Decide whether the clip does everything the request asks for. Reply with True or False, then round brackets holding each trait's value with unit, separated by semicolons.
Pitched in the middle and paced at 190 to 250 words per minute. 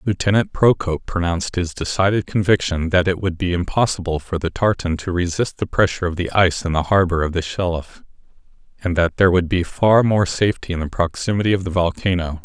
False (90 Hz; 200 wpm)